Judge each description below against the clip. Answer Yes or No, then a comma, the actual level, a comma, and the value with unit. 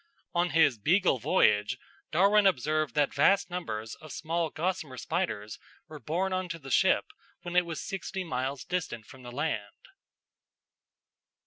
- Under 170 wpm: Yes, average, 145 wpm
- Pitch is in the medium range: Yes, medium, 155 Hz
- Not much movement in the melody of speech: No, wide, 5.6 semitones